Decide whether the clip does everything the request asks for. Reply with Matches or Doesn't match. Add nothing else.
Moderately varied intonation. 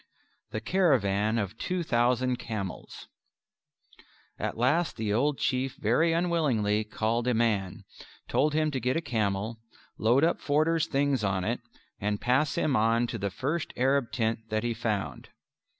Matches